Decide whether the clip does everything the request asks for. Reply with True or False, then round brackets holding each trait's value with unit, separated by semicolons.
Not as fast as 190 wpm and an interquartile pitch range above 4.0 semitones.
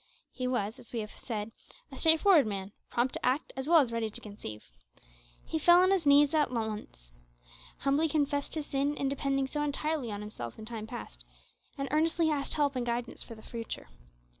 False (195 wpm; 5.2 semitones)